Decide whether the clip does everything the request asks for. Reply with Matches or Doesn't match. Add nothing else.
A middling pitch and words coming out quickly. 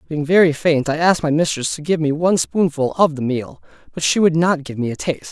Matches